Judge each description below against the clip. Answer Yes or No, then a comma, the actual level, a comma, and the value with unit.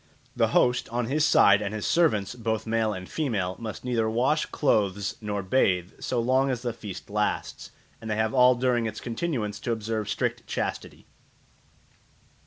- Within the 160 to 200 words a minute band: Yes, average, 170 wpm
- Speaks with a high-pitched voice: No, low, 110 Hz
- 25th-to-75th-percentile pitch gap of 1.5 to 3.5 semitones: Yes, average, 3.1 semitones